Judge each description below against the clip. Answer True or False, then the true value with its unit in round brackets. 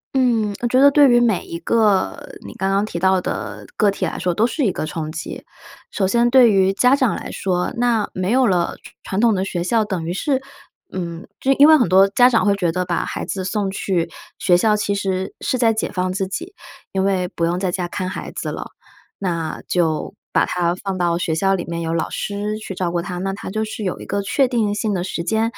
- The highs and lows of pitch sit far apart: False (3.7 semitones)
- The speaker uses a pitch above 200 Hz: False (195 Hz)